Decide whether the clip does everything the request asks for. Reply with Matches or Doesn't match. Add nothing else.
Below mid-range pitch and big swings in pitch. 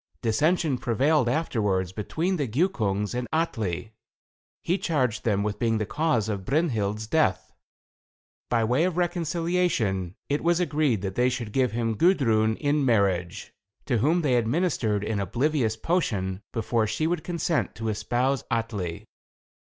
Matches